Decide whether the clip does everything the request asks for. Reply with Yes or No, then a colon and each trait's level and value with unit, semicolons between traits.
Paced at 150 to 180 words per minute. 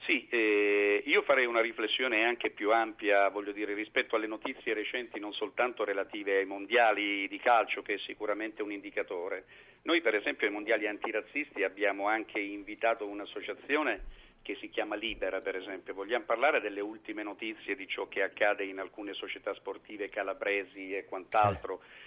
Yes: average, 160 wpm